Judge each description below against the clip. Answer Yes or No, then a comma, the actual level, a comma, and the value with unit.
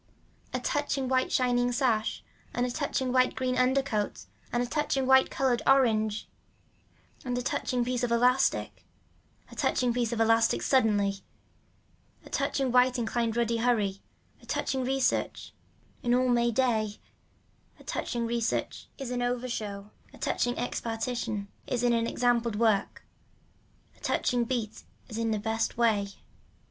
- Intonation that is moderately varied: No, narrow, 2.0 semitones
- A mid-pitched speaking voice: No, high, 240 Hz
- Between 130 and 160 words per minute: Yes, average, 150 wpm